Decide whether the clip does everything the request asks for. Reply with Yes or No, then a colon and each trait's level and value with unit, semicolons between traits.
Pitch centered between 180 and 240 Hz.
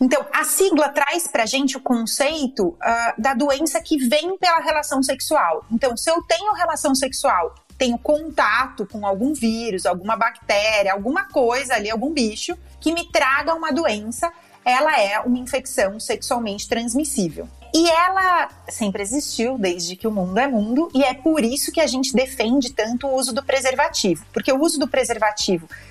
No: very high, 270 Hz